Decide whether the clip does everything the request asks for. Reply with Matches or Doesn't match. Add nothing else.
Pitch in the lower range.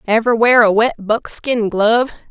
Doesn't match